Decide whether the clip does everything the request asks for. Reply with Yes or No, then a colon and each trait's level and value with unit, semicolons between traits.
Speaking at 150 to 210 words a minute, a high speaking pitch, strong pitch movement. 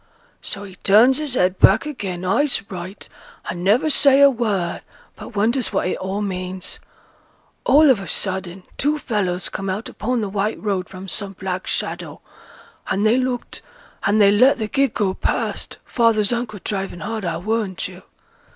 No: average, 170 wpm; high, 205 Hz; average, 4.2 semitones